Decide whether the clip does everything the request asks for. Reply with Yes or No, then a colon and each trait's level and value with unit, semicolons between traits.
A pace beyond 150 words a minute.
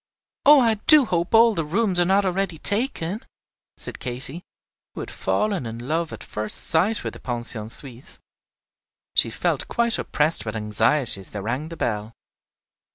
Yes: average, 165 wpm